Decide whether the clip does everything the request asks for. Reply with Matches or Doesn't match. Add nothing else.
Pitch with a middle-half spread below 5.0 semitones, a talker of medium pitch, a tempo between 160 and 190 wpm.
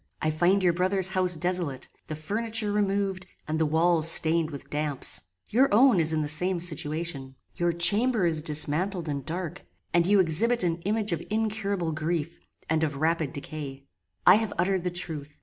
Matches